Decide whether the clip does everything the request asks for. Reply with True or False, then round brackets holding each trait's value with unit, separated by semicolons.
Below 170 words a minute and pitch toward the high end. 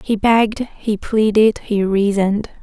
True (135 wpm; 210 Hz)